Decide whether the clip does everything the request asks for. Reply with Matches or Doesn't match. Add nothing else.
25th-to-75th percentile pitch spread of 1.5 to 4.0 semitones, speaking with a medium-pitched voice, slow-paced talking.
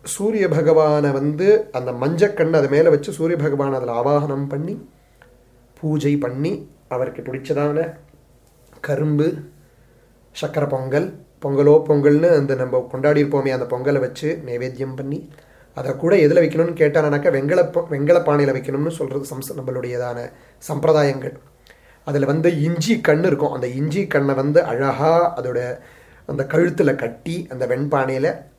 Matches